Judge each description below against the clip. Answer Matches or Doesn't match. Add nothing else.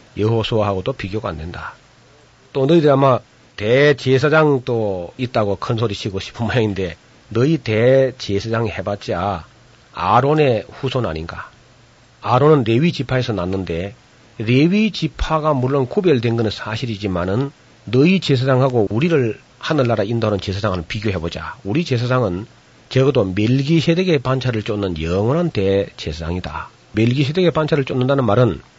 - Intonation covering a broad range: Doesn't match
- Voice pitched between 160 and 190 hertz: Doesn't match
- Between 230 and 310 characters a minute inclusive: Doesn't match